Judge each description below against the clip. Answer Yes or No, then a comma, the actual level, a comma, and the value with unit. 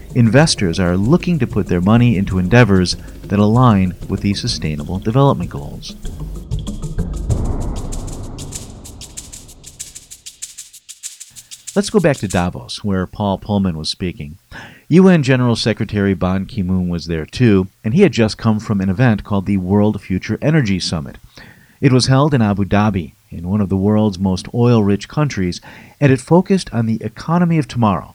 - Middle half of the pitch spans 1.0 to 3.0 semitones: No, average, 4.5 semitones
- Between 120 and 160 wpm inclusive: Yes, average, 155 wpm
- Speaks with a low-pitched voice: Yes, low, 105 Hz